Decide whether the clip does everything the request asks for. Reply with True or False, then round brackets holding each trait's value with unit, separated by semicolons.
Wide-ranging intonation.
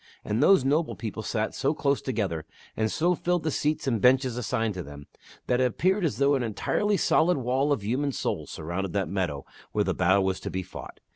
True (6.7 semitones)